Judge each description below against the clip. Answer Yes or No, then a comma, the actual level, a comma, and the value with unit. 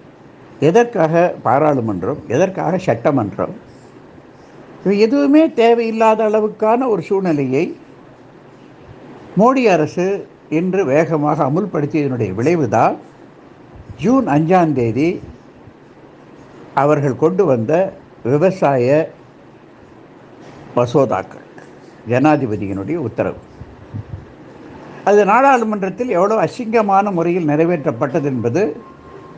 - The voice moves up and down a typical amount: No, wide, 6.8 semitones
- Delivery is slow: Yes, slow, 65 wpm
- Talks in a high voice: No, medium, 170 Hz